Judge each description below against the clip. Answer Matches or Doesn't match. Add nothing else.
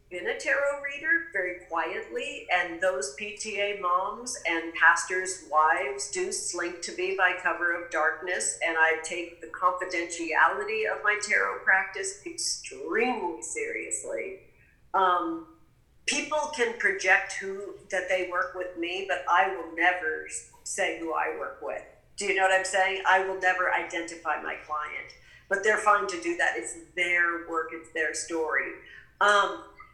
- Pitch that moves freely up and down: Matches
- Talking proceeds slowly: Doesn't match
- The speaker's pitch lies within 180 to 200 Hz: Matches